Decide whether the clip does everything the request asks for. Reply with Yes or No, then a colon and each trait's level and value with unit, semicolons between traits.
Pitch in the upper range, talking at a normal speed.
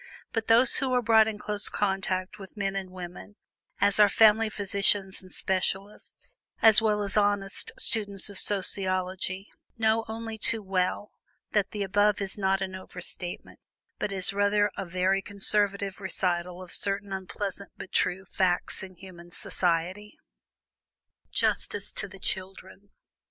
Yes: high, 195 Hz; average, 145 wpm